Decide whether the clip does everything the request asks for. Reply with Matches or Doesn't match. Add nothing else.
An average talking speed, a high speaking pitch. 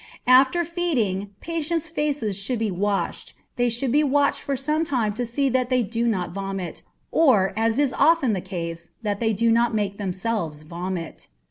Matches